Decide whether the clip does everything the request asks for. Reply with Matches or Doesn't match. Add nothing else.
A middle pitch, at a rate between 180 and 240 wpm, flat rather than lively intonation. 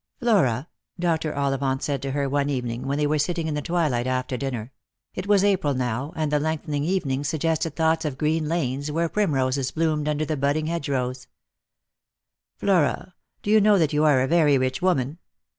Doesn't match